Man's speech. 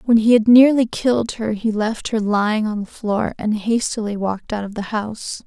No: female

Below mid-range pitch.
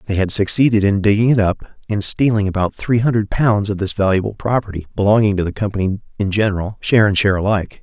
Yes: low, 100 Hz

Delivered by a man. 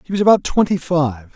Yes: male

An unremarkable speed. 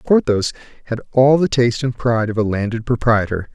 Yes: average, 185 wpm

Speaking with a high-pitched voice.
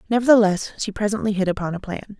Yes: high, 205 Hz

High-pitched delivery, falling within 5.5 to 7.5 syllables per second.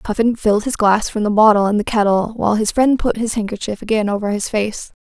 Yes: high, 215 Hz; 6.0 syllables/s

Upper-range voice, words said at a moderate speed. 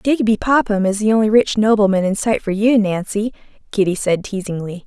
Yes: high, 210 Hz; average, 185 wpm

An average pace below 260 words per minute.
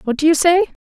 No: fast, 275 wpm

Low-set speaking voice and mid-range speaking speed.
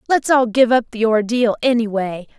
No: high, 230 Hz; average, 175 wpm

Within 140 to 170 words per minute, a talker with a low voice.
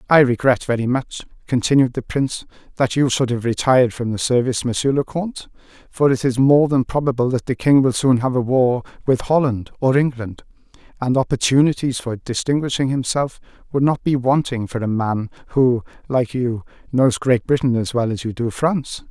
No: average, 190 wpm; low, 125 Hz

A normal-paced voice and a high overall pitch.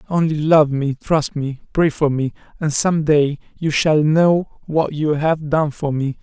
No: average, 195 wpm; medium, 150 Hz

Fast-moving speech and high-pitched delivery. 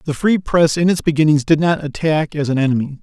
No: fast, 240 wpm; medium, 155 Hz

